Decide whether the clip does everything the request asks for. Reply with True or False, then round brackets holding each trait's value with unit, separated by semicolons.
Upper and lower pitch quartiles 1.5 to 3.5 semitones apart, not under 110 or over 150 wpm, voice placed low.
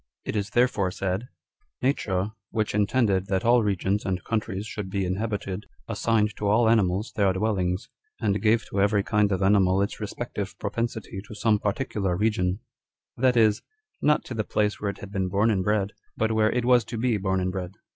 False (2.6 semitones; 205 wpm; 105 Hz)